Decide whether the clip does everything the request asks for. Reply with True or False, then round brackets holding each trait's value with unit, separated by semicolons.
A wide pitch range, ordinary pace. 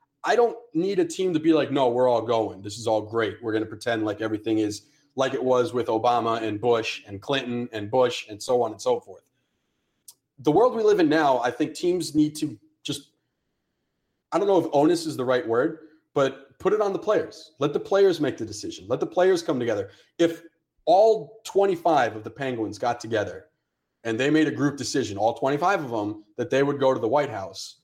False (6.6 semitones; 225 wpm)